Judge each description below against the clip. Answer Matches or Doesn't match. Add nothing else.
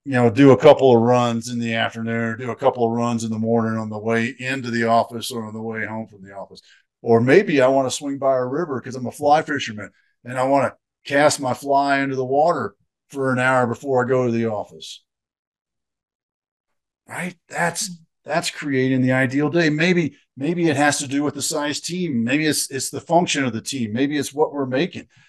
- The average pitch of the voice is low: Matches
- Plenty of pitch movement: Doesn't match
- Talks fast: Matches